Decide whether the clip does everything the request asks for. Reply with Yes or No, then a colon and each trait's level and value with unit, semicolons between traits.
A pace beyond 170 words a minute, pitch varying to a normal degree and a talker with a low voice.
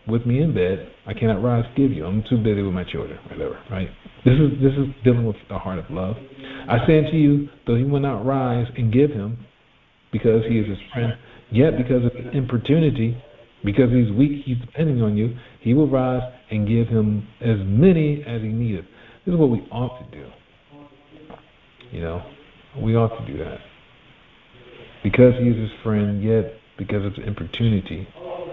Yes: average, 190 wpm; average, 3.7 semitones; low, 120 Hz